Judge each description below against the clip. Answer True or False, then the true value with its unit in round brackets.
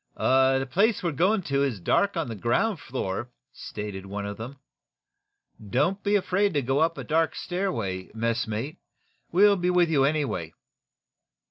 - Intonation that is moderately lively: False (8.0 semitones)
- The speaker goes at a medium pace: True (155 wpm)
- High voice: False (140 Hz)